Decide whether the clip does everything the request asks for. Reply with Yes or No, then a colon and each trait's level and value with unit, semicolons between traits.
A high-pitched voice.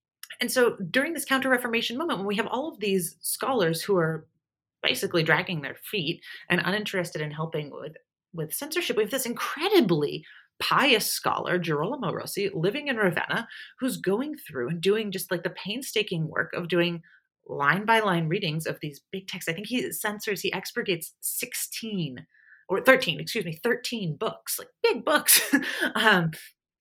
Yes: high, 195 Hz